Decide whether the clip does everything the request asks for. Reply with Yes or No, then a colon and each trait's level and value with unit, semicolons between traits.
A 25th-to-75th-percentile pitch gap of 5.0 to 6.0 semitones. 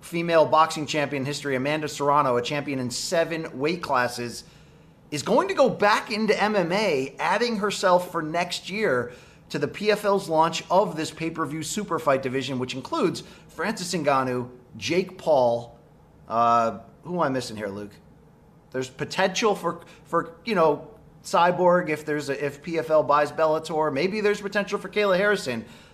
No: average, 4.2 semitones